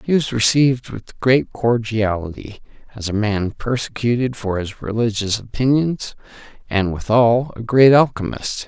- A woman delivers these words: No, male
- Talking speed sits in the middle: No, slow, 130 wpm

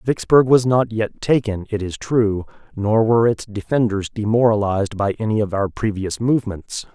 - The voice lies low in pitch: Yes, low, 110 Hz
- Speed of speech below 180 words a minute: Yes, average, 165 wpm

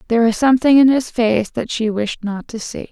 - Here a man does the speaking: No, female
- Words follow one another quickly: Yes, fast, 270 wpm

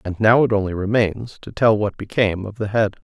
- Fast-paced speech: Yes, fast, 230 wpm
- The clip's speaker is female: No, male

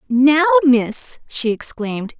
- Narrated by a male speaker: No, female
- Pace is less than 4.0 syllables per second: Yes, 3.5 syllables/s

